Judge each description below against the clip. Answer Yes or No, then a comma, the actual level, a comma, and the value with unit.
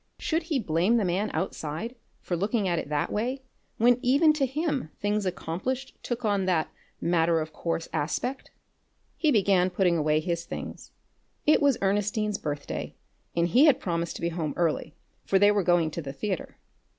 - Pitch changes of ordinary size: No, wide, 6.2 semitones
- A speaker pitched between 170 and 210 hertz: Yes, high, 190 Hz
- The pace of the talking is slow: No, average, 175 wpm